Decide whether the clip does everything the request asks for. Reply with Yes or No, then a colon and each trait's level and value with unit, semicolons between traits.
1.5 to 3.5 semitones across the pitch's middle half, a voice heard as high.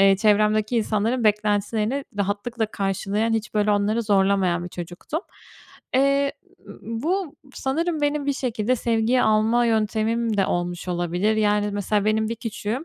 Yes: narrow, 2.6 semitones; high, 215 Hz